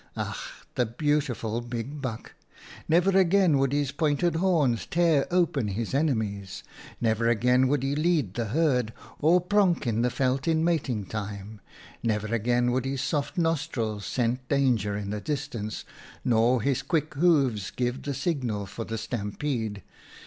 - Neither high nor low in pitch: No, low, 130 Hz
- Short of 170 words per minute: Yes, average, 155 wpm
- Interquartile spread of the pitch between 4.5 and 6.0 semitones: Yes, average, 5.1 semitones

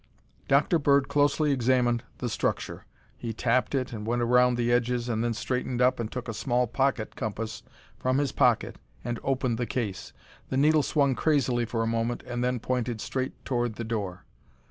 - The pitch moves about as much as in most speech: No, narrow, 2.1 semitones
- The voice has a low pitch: Yes, low, 120 Hz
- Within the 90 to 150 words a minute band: No, average, 185 wpm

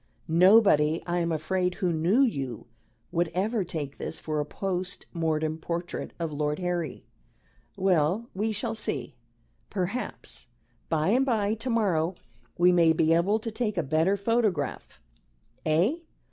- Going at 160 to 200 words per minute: No, average, 145 wpm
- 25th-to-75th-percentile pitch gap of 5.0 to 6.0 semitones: No, average, 4.6 semitones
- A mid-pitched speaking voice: Yes, medium, 180 Hz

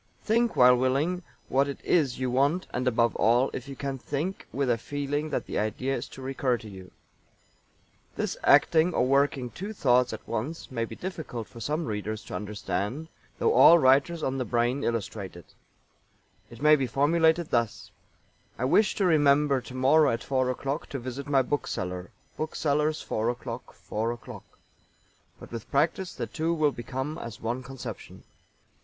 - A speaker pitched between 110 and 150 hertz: Yes, low, 135 Hz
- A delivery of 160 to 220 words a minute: Yes, average, 170 wpm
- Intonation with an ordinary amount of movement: Yes, average, 4.1 semitones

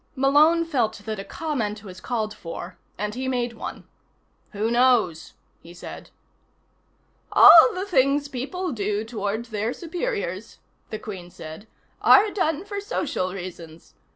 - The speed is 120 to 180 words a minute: Yes, slow, 135 wpm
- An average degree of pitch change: No, wide, 6.2 semitones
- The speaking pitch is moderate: No, high, 225 Hz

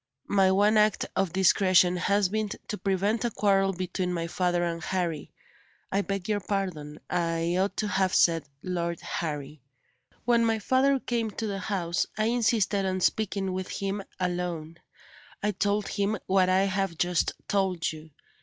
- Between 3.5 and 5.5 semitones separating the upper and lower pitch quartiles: No, narrow, 2.6 semitones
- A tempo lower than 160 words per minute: No, average, 165 wpm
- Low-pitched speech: No, high, 190 Hz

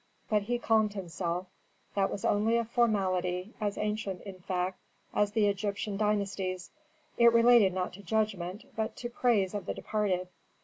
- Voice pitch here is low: No, high, 205 Hz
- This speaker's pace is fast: No, average, 160 wpm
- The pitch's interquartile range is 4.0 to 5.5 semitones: No, average, 2.7 semitones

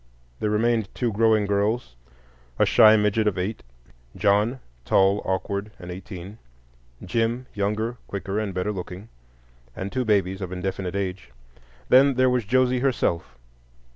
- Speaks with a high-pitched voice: No, low, 105 Hz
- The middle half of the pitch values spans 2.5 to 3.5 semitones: Yes, average, 3.0 semitones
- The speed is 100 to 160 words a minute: Yes, average, 140 wpm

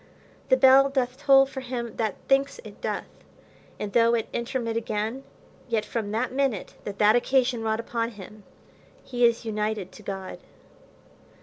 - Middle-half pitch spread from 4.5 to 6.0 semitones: No, average, 3.2 semitones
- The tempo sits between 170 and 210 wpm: No, average, 160 wpm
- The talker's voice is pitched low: No, high, 230 Hz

